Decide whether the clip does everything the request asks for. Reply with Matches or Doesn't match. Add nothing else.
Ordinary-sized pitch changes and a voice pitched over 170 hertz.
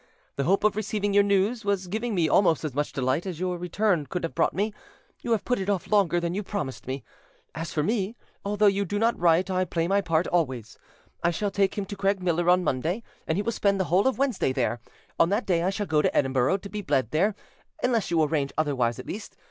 Matches